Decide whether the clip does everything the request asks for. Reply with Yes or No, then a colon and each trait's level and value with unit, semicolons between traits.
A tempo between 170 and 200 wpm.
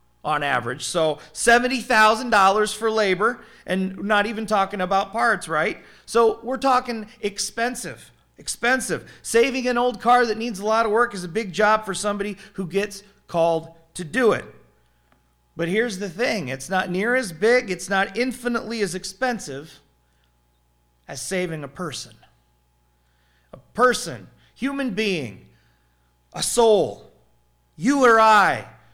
No: average, 140 wpm